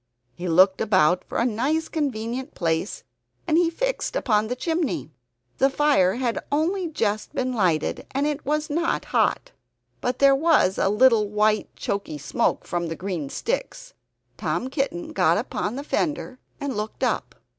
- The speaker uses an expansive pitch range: Yes, wide, 6.9 semitones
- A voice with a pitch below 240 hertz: No, very high, 255 Hz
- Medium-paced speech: Yes, average, 155 wpm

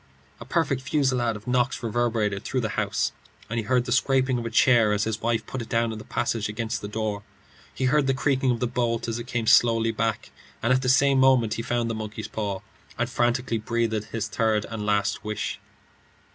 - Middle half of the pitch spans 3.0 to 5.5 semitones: No, narrow, 2.4 semitones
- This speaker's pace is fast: Yes, fast, 215 wpm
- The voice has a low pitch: Yes, low, 115 Hz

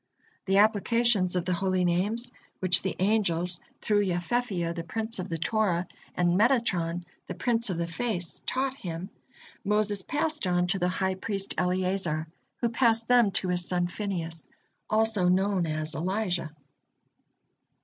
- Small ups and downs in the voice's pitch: No, average, 3.8 semitones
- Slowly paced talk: No, average, 150 wpm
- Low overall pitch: No, high, 190 Hz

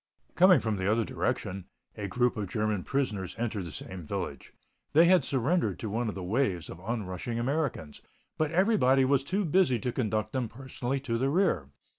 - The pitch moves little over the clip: No, wide, 5.5 semitones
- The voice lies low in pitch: Yes, low, 120 Hz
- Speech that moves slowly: No, average, 185 wpm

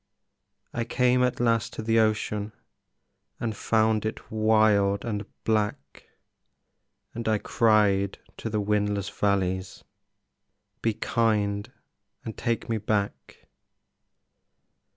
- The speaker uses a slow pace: Yes, slow, 105 wpm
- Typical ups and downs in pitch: No, narrow, 1.8 semitones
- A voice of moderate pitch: No, low, 110 Hz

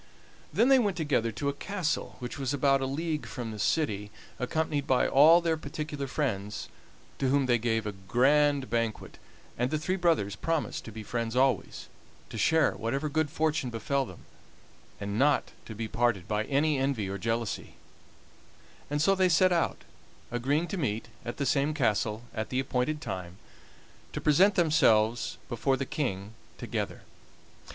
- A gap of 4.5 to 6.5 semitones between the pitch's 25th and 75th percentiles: Yes, average, 5.3 semitones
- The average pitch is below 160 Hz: Yes, low, 135 Hz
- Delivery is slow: No, average, 165 wpm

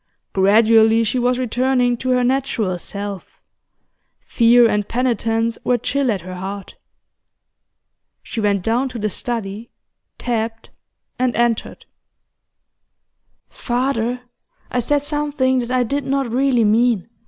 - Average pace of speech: No, slow, 120 wpm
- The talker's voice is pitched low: No, high, 235 Hz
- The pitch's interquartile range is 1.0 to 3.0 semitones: Yes, narrow, 2.6 semitones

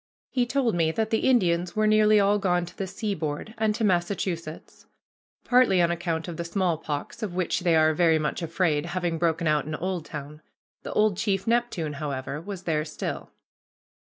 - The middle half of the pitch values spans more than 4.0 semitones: Yes, average, 4.4 semitones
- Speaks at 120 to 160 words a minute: No, average, 180 wpm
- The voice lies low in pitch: No, medium, 175 Hz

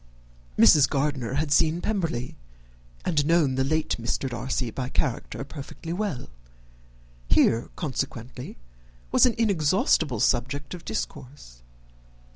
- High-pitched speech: No, medium, 140 Hz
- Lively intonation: No, average, 4.2 semitones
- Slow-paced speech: Yes, slow, 110 wpm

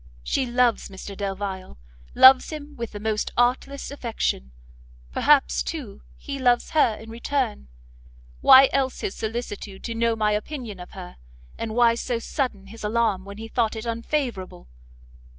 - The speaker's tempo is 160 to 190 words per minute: No, average, 150 wpm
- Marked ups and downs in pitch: No, average, 3.7 semitones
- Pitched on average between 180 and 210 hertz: No, high, 225 Hz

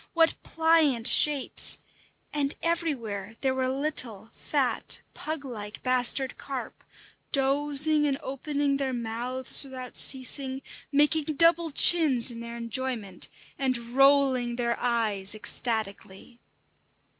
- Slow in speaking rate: Yes, slow, 110 wpm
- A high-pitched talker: Yes, very high, 260 Hz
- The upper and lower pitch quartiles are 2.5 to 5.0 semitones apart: Yes, average, 3.6 semitones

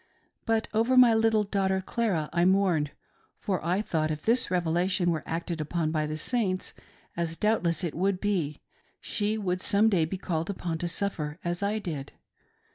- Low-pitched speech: No, medium, 180 Hz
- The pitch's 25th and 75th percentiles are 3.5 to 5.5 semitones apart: Yes, average, 3.9 semitones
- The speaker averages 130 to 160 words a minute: No, average, 175 wpm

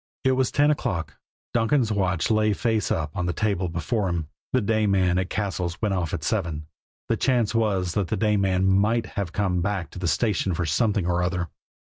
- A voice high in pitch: No, very low, 95 Hz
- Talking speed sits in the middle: No, fast, 210 wpm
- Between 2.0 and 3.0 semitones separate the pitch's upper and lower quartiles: No, average, 3.6 semitones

